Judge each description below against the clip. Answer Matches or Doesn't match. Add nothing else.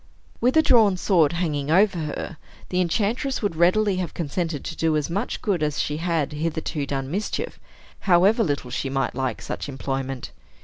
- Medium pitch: Matches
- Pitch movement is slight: Doesn't match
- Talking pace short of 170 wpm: Doesn't match